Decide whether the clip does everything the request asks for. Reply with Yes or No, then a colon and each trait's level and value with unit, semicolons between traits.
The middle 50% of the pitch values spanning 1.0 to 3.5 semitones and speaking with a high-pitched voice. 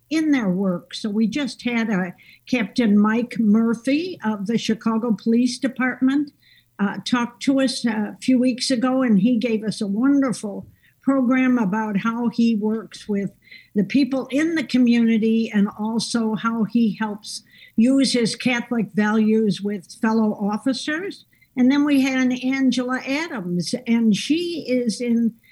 Yes: average, 3.0 semitones; high, 230 Hz